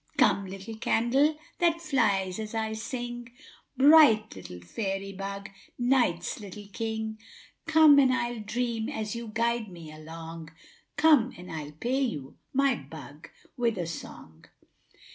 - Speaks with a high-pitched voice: Yes, high, 220 Hz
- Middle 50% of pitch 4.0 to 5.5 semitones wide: Yes, average, 5.0 semitones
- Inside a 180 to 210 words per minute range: No, average, 140 wpm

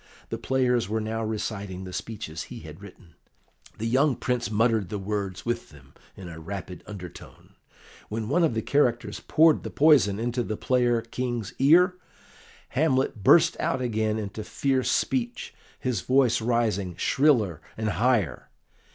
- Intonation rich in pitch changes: No, average, 4.2 semitones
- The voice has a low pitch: Yes, low, 115 Hz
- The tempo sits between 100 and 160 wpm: Yes, average, 150 wpm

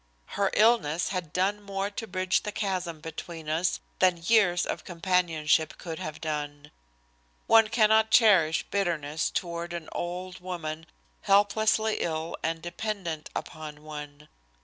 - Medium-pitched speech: Yes, medium, 175 Hz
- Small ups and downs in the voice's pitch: No, average, 4.0 semitones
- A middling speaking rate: No, slow, 130 wpm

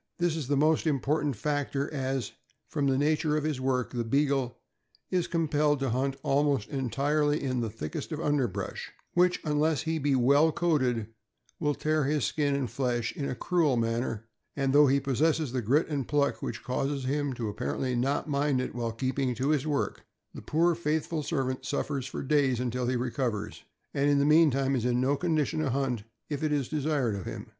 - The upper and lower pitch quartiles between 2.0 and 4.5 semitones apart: Yes, average, 2.9 semitones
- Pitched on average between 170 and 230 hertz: No, medium, 140 Hz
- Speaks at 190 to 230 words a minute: Yes, average, 195 wpm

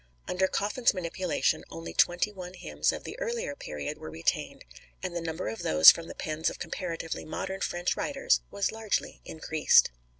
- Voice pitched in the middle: Yes, medium, 175 Hz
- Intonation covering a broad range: No, average, 4.2 semitones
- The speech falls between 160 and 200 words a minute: Yes, average, 170 wpm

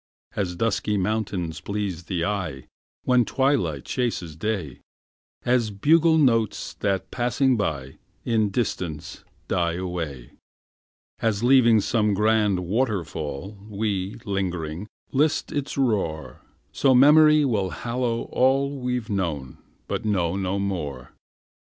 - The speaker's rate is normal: No, slow, 115 wpm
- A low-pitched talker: Yes, low, 105 Hz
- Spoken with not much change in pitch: No, wide, 5.6 semitones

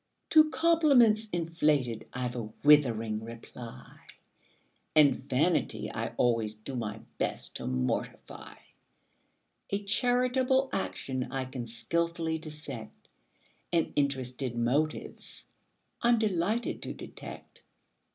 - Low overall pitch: No, medium, 145 Hz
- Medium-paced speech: No, slow, 100 wpm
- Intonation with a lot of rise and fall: Yes, wide, 8.8 semitones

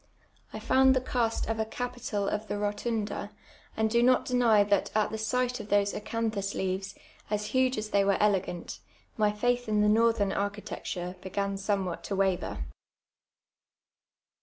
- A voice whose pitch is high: Yes, high, 210 Hz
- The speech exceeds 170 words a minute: No, average, 160 wpm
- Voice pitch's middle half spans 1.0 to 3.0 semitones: Yes, narrow, 2.5 semitones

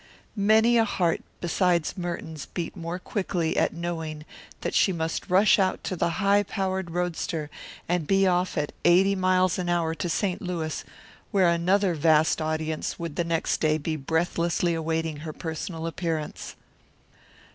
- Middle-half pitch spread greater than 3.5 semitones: No, narrow, 2.4 semitones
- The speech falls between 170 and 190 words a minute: No, average, 155 wpm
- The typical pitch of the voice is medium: Yes, medium, 170 Hz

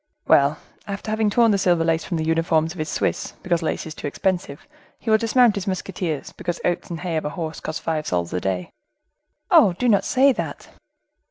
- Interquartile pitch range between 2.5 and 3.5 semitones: No, average, 4.1 semitones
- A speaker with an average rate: No, fast, 210 wpm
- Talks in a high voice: No, medium, 175 Hz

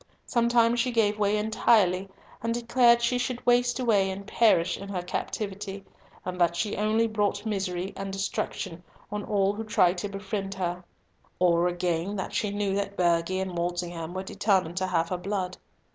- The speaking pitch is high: Yes, high, 195 Hz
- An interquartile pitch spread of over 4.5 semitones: No, average, 3.1 semitones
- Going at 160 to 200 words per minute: Yes, average, 175 wpm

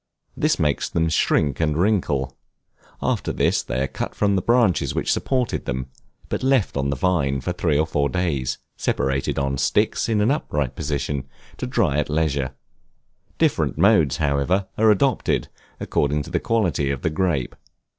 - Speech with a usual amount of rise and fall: No, wide, 5.7 semitones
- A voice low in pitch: Yes, very low, 75 Hz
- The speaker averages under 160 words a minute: No, average, 165 wpm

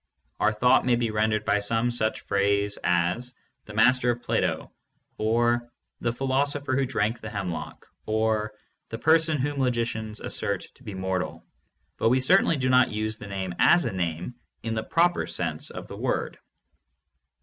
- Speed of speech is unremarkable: Yes, average, 170 wpm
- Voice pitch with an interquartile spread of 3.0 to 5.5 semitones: Yes, average, 3.6 semitones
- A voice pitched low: Yes, low, 115 Hz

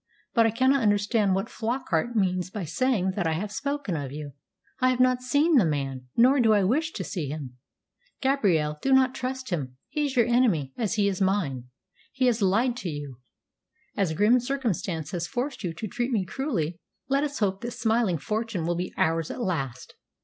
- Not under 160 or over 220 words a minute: Yes, average, 200 wpm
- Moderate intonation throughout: No, wide, 7.2 semitones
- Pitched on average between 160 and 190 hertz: No, high, 205 Hz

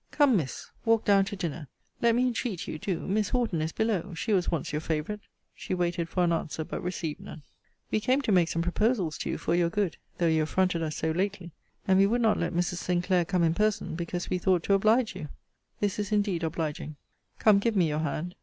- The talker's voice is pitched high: No, medium, 180 Hz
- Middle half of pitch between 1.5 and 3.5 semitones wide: No, average, 4.0 semitones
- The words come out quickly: Yes, fast, 230 wpm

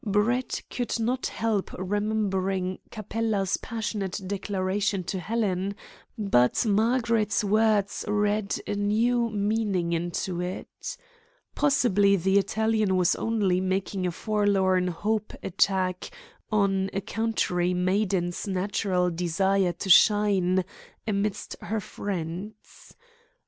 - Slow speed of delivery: Yes, slow, 100 wpm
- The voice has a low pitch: No, high, 200 Hz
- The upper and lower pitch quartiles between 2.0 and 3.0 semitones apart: Yes, narrow, 2.5 semitones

